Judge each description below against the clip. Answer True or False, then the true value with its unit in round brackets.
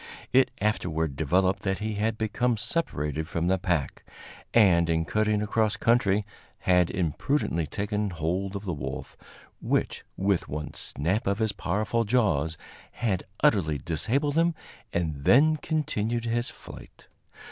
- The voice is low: True (100 Hz)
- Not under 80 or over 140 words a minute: True (135 wpm)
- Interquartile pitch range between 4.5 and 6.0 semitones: True (5.2 semitones)